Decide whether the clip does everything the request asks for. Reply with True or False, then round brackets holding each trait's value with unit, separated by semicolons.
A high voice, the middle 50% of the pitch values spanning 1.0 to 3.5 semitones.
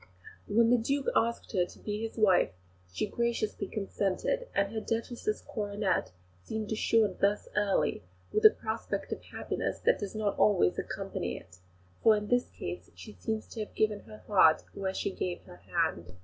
True (210 Hz; 3.0 semitones)